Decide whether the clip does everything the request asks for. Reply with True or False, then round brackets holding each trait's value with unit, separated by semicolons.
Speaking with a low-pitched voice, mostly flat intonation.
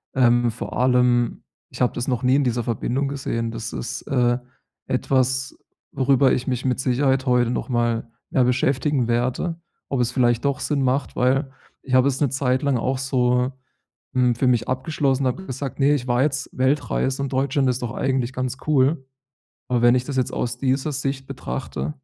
True (130 Hz; 1.7 semitones)